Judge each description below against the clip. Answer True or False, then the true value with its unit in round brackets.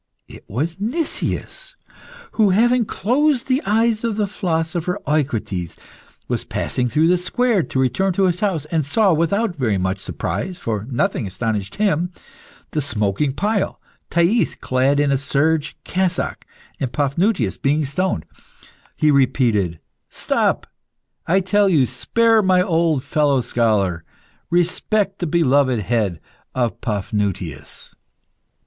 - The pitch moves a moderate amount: False (7.9 semitones)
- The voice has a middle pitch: True (155 Hz)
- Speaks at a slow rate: True (130 wpm)